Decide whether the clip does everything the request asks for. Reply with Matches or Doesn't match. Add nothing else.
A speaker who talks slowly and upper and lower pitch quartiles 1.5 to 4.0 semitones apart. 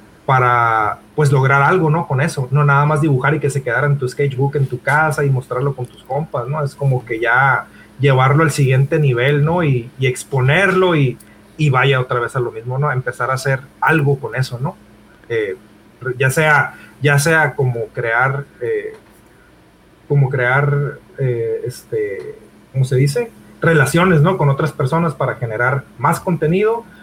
Doesn't match